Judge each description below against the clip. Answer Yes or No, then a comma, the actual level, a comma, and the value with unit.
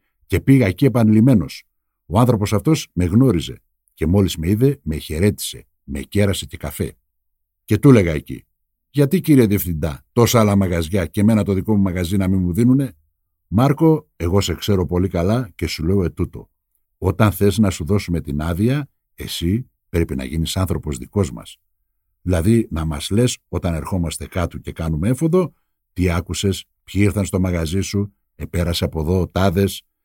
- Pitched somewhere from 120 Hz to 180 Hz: No, very low, 95 Hz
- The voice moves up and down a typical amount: Yes, average, 4.4 semitones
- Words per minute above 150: Yes, fast, 170 wpm